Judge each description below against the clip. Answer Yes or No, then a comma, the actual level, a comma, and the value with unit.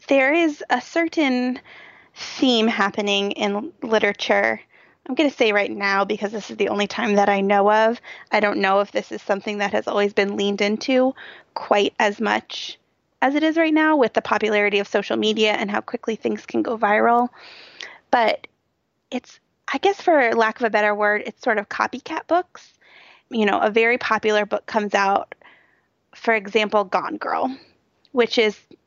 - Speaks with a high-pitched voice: Yes, high, 220 Hz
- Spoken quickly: No, average, 180 wpm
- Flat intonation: No, average, 3.9 semitones